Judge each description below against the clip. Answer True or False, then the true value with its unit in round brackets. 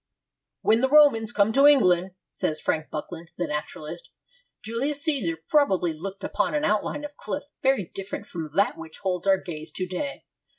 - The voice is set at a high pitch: True (195 Hz)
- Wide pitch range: True (8.0 semitones)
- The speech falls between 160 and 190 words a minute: True (170 wpm)